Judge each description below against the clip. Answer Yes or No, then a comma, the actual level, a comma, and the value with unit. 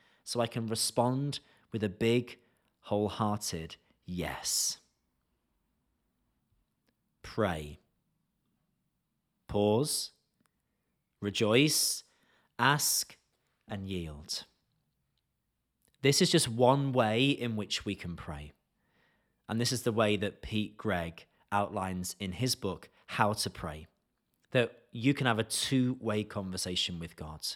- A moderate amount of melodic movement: Yes, average, 5.0 semitones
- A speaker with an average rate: No, slow, 110 wpm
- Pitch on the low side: Yes, low, 105 Hz